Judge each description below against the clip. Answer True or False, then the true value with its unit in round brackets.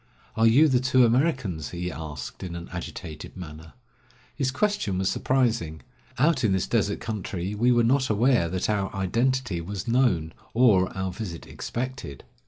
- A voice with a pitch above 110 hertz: False (105 Hz)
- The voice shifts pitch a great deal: True (6.2 semitones)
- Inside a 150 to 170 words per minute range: True (160 wpm)